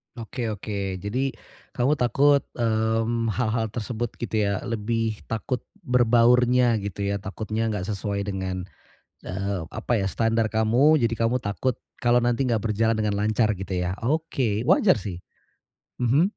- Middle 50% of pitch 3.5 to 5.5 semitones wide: No, average, 2.9 semitones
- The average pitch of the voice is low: Yes, low, 115 Hz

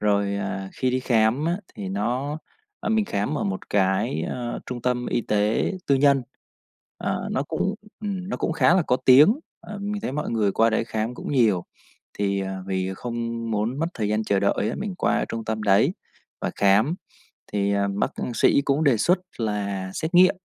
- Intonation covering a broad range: Yes, wide, 6.0 semitones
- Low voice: Yes, low, 115 Hz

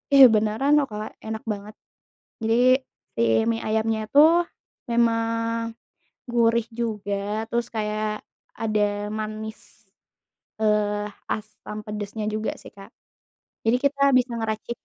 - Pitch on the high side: Yes, high, 220 Hz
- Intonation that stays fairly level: Yes, narrow, 1.7 semitones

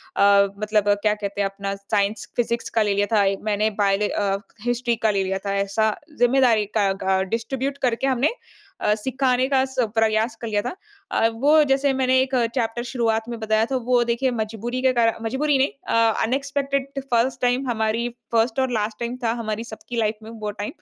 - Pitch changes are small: No, average, 3.3 semitones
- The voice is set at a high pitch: Yes, high, 230 Hz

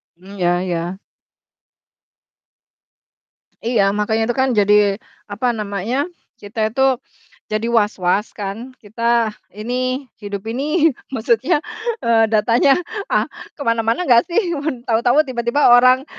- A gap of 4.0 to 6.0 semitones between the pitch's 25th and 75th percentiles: No, average, 3.6 semitones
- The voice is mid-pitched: No, high, 230 Hz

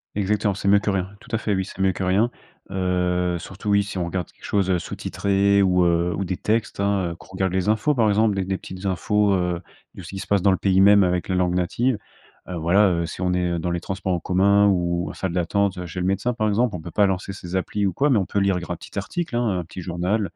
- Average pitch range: No, narrow, 2.2 semitones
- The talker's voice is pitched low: Yes, very low, 95 Hz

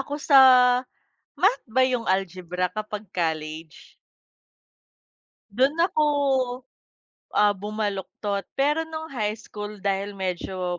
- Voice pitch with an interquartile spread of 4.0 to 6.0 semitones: Yes, wide, 5.6 semitones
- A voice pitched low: No, high, 205 Hz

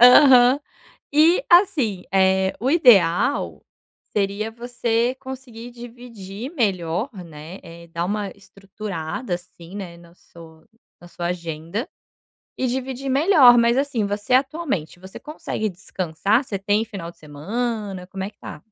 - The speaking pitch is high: Yes, high, 210 Hz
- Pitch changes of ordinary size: No, wide, 5.7 semitones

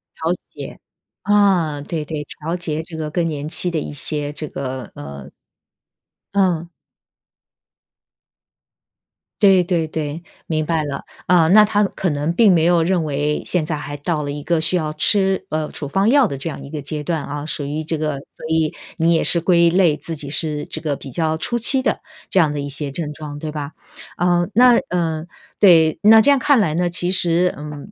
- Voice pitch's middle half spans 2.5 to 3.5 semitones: Yes, average, 3.1 semitones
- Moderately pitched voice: Yes, medium, 160 Hz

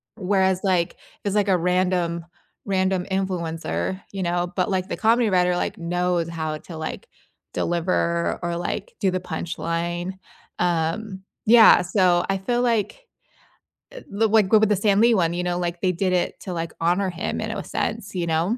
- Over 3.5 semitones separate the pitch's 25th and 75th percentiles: No, narrow, 2.4 semitones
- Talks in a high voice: No, medium, 180 Hz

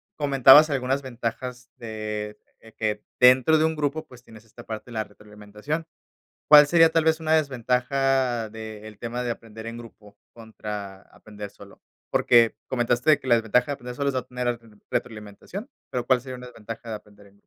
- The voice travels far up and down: No, average, 3.8 semitones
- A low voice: Yes, low, 120 Hz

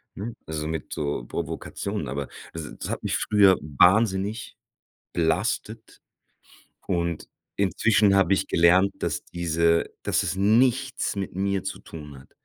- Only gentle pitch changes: No, average, 3.8 semitones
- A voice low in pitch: Yes, very low, 95 Hz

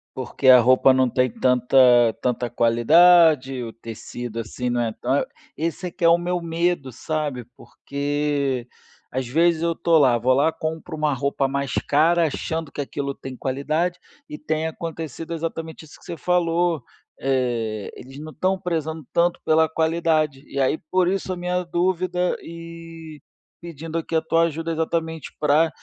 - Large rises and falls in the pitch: No, average, 4.0 semitones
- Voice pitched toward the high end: No, medium, 155 Hz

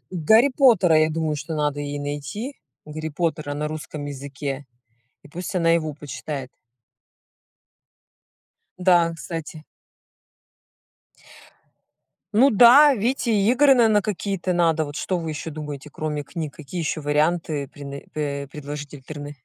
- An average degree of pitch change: Yes, average, 3.7 semitones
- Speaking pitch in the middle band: Yes, medium, 155 Hz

